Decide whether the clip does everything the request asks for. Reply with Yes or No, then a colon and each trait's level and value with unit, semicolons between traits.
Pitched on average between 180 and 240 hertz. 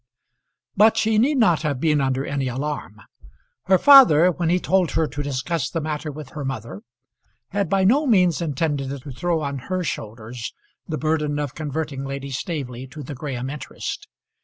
No: medium, 150 Hz